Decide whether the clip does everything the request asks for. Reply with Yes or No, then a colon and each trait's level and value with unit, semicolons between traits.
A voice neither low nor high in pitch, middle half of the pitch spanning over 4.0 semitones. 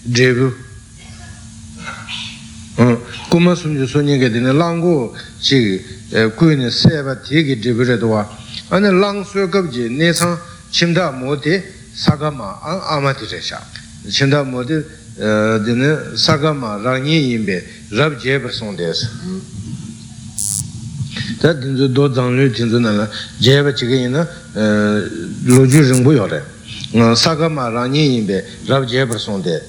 No: low, 130 Hz; average, 5.2 semitones